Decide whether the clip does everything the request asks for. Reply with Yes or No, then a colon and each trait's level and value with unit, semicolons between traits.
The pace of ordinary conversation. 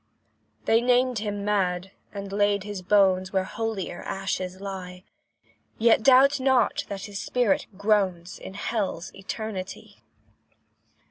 No: slow, 120 wpm